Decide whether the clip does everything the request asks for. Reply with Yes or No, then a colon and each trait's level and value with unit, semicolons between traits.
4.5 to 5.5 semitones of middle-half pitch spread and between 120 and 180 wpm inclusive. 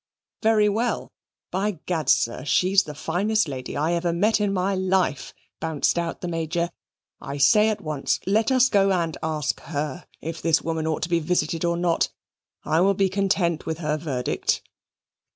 No: average, 3.7 semitones; average, 175 wpm